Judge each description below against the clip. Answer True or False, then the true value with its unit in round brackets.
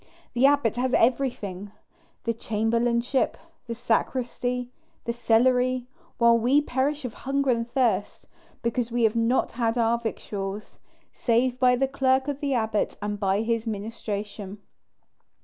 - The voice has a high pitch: True (235 Hz)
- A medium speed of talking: False (130 wpm)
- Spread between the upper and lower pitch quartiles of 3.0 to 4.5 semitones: False (2.4 semitones)